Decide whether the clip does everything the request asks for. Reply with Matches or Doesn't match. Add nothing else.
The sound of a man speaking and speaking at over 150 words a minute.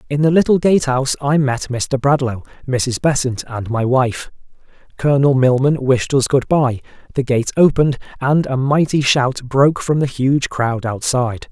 Matches